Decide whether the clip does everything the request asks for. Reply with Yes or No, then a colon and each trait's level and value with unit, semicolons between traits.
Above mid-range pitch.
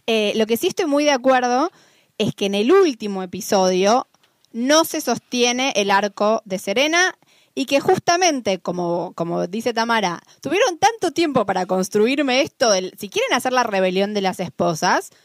Yes: high, 230 Hz